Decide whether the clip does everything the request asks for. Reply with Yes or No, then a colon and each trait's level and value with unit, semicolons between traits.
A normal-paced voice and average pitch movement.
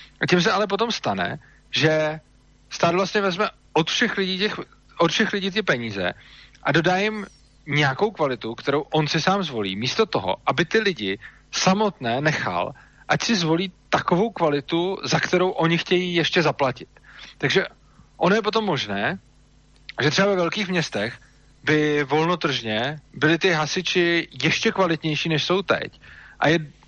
Yes: average, 150 wpm; average, 4.7 semitones